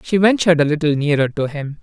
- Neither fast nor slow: No, fast, 230 wpm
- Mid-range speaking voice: Yes, medium, 155 Hz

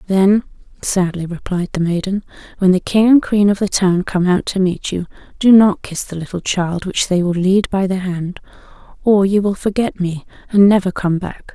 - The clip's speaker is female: Yes, female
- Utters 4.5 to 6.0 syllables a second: Yes, 4.9 syllables/s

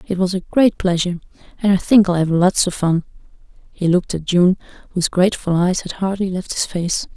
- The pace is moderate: No, fast, 210 wpm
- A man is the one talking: No, female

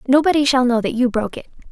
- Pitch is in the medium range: No, very high, 255 Hz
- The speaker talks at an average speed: No, fast, 245 wpm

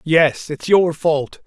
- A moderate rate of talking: Yes, average, 165 wpm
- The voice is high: No, medium, 160 Hz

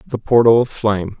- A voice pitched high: No, low, 110 Hz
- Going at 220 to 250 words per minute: No, average, 200 wpm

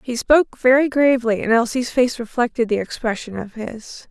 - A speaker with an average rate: Yes, average, 175 wpm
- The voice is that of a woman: Yes, female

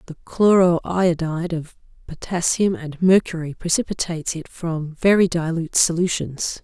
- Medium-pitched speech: Yes, medium, 170 Hz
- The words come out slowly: Yes, slow, 120 wpm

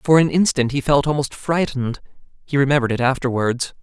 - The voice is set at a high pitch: No, medium, 140 Hz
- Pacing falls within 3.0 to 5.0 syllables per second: No, 6.2 syllables/s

